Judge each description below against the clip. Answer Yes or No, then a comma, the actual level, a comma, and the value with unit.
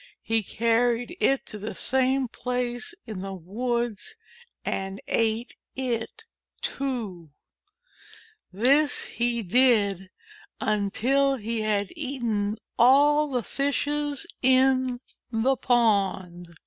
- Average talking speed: No, slow, 95 wpm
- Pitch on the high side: Yes, high, 240 Hz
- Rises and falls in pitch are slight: No, average, 4.0 semitones